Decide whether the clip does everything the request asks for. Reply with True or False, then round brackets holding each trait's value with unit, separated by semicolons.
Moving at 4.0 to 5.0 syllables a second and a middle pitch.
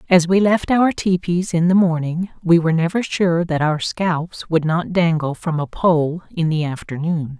True (4.5 syllables/s; 170 Hz)